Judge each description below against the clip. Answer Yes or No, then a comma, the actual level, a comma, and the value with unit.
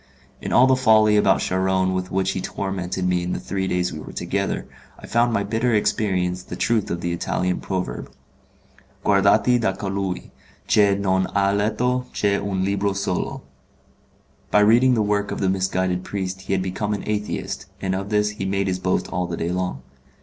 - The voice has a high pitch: No, very low, 95 Hz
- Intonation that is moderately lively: No, narrow, 2.1 semitones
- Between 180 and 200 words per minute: Yes, average, 190 wpm